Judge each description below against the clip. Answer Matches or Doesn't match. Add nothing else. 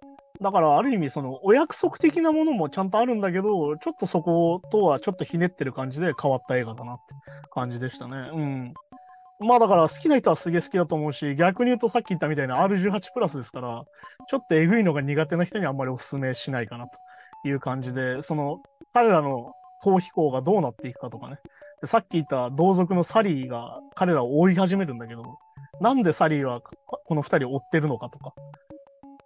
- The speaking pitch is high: Doesn't match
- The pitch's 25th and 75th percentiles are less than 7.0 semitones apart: Doesn't match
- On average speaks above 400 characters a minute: Matches